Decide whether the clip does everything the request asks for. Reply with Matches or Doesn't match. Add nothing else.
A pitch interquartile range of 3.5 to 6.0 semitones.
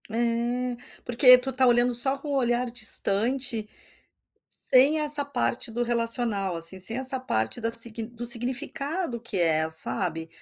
Doesn't match